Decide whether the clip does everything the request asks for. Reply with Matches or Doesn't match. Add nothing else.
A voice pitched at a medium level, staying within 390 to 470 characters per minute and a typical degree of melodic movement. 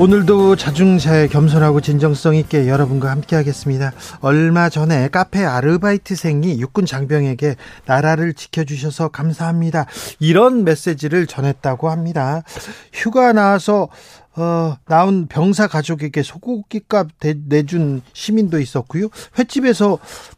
Doesn't match